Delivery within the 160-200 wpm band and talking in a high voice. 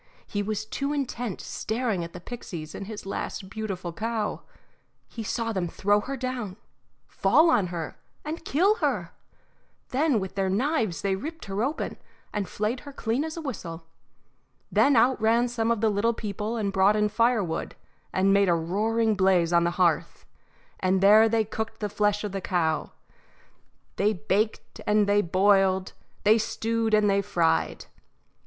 Yes: average, 170 wpm; high, 210 Hz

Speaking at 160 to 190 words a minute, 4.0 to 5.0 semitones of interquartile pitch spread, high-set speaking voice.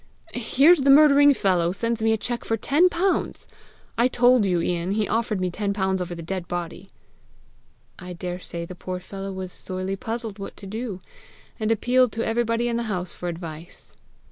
Yes: average, 185 wpm; average, 4.7 semitones; high, 200 Hz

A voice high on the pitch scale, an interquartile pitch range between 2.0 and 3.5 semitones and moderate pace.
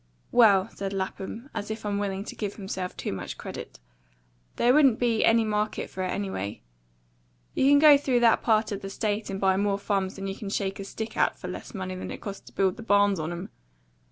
No: high, 200 Hz; narrow, 2.4 semitones; fast, 220 wpm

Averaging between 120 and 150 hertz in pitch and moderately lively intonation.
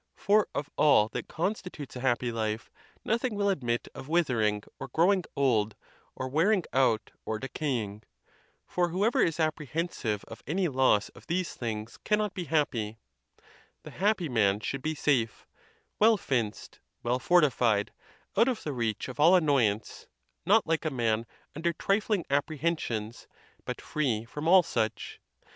No: medium, 140 Hz; wide, 7.3 semitones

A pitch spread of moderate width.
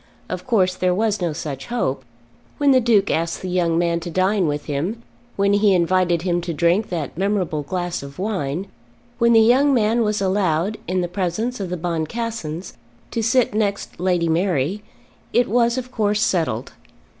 Yes: average, 4.3 semitones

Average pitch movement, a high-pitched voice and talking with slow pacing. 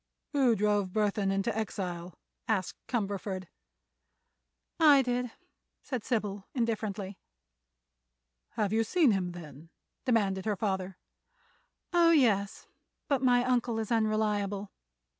Yes: average, 3.6 semitones; high, 210 Hz; slow, 105 wpm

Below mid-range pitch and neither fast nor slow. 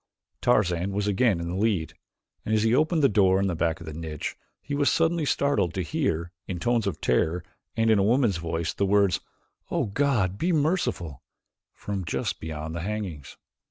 Yes: low, 100 Hz; average, 195 wpm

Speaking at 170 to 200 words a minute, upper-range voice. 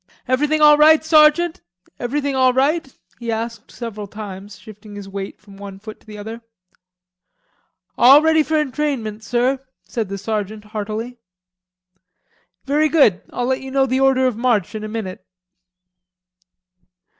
No: average, 145 wpm; high, 240 Hz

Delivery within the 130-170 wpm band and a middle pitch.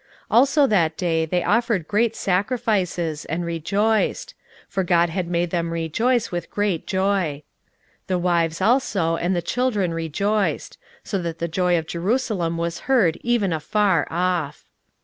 Yes: average, 150 wpm; medium, 180 Hz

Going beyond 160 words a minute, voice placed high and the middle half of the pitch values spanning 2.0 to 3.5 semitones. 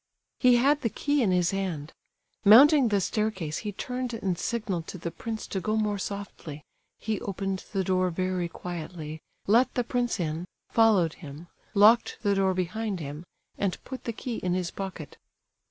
No: average, 170 wpm; high, 195 Hz; average, 4.2 semitones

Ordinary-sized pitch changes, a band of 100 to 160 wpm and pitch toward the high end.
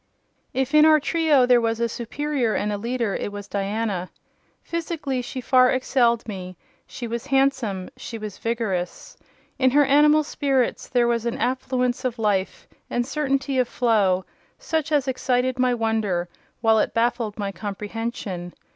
Yes: average, 3.9 semitones; average, 155 wpm; high, 240 Hz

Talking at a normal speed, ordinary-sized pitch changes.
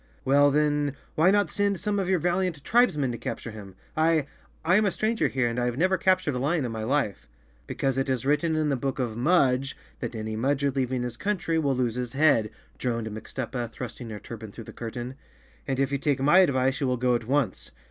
No: fast, 230 wpm; average, 4.6 semitones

